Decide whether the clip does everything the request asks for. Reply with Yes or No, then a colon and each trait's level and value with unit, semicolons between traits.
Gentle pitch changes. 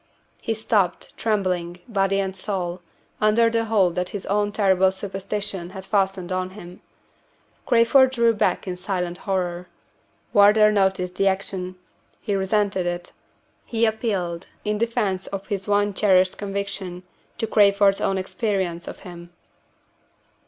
Yes: narrow, 2.2 semitones